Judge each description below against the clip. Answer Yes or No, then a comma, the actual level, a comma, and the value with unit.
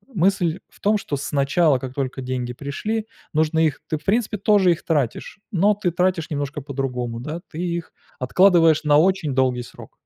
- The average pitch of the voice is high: No, medium, 155 Hz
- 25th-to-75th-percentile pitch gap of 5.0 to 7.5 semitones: Yes, average, 5.3 semitones